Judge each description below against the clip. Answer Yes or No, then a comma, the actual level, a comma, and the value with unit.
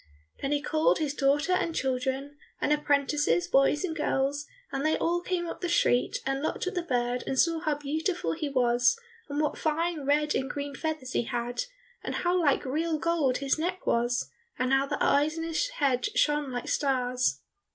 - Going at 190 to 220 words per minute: Yes, average, 195 wpm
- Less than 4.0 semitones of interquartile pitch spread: Yes, average, 3.2 semitones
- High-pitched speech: Yes, very high, 290 Hz